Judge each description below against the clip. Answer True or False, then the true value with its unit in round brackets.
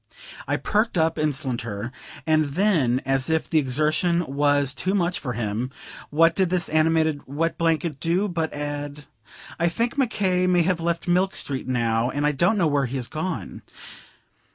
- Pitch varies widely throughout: False (4.1 semitones)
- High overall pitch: False (155 Hz)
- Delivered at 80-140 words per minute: False (175 wpm)